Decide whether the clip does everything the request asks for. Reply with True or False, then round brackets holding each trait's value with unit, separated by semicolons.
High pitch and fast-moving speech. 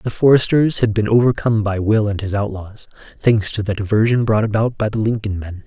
False (110 Hz; 210 wpm)